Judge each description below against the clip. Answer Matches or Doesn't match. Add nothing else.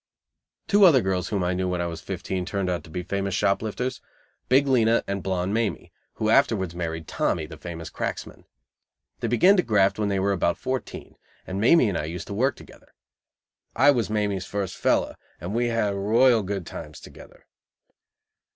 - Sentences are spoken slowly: Doesn't match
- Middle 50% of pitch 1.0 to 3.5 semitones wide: Doesn't match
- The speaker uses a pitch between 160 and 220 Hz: Doesn't match